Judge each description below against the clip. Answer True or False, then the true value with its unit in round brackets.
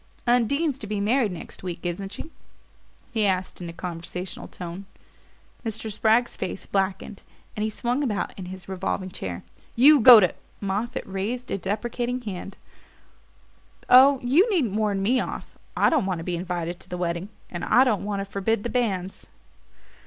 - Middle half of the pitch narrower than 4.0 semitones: False (4.5 semitones)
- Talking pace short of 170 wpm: False (175 wpm)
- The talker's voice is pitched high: True (200 Hz)